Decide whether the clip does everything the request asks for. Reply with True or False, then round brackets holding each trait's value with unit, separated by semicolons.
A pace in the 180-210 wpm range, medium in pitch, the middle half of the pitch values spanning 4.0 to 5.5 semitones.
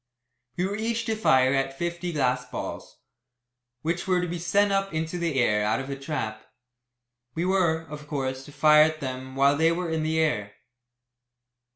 True (185 wpm; 155 Hz; 4.6 semitones)